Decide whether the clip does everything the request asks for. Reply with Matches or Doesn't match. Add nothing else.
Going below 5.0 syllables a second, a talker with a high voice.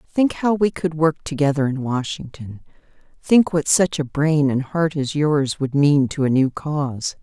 Doesn't match